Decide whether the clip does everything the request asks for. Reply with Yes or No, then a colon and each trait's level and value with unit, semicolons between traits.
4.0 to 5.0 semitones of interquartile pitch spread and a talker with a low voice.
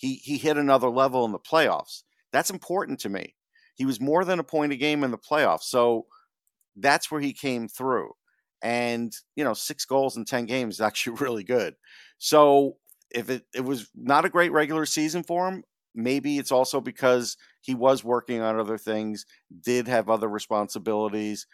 Yes: average, 4.3 semitones; low, 130 Hz